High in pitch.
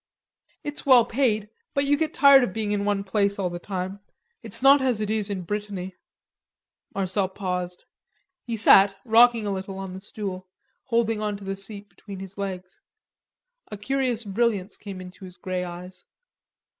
Yes: high, 200 Hz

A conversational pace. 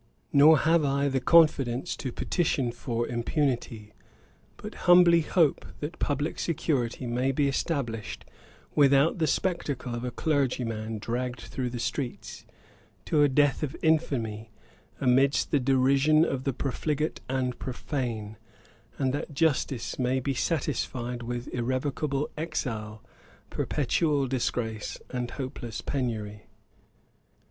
No: slow, 120 wpm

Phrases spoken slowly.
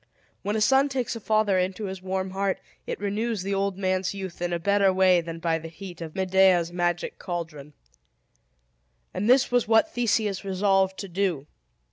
No: average, 180 wpm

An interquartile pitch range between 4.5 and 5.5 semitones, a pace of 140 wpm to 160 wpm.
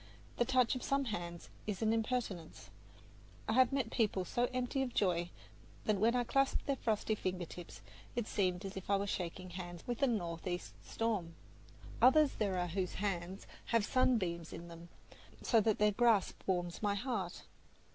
No: average, 5.2 semitones; average, 175 wpm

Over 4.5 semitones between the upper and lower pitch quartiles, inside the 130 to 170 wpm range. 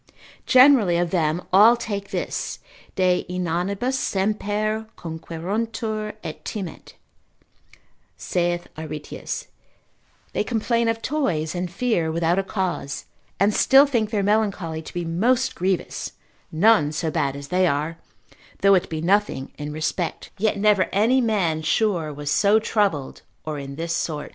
Yes: average, 5.0 semitones; average, 140 wpm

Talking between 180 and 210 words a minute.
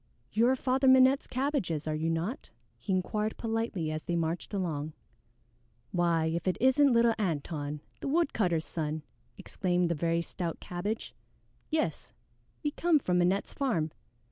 No: average, 145 wpm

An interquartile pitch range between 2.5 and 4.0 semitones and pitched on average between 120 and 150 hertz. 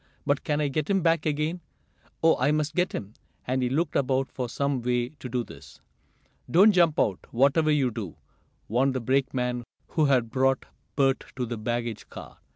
Yes: average, 3.7 semitones; low, 135 Hz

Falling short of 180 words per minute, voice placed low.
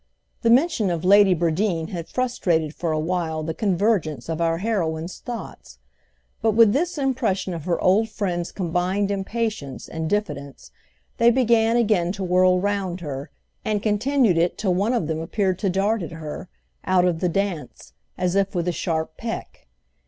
No: average, 170 wpm; medium, 185 Hz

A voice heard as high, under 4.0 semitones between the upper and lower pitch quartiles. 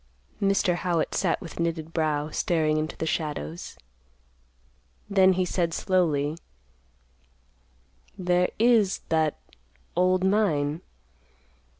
No: medium, 170 Hz; average, 3.1 semitones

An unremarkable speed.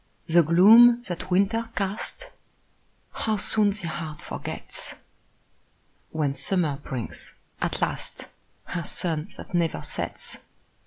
No: slow, 110 wpm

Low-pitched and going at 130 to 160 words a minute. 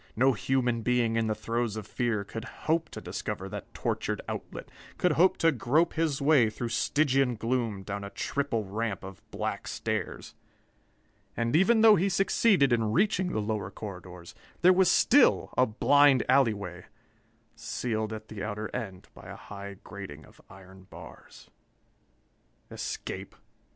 Yes: low, 115 Hz; average, 155 wpm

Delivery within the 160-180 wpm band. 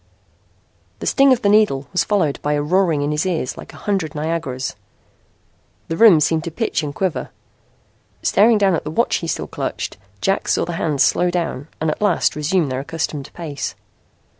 No: average, 190 wpm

